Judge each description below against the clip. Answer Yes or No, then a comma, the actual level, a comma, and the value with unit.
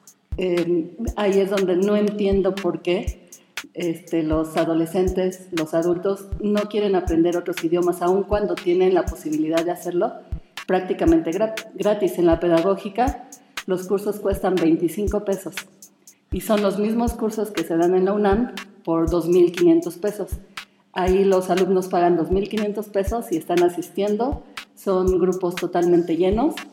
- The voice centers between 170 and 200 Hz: Yes, high, 190 Hz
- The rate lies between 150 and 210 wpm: No, average, 140 wpm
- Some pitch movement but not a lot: Yes, average, 3.0 semitones